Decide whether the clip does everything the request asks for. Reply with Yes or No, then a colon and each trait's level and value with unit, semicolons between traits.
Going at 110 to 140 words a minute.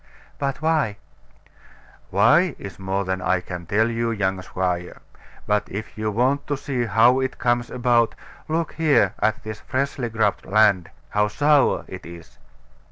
No: average, 150 wpm